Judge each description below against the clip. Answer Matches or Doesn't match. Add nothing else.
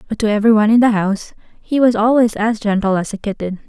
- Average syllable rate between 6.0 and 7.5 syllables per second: Matches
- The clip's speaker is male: Doesn't match